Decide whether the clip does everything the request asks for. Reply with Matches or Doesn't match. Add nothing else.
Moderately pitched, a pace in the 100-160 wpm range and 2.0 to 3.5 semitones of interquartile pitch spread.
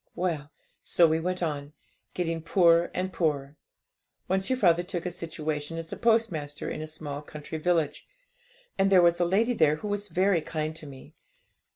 Doesn't match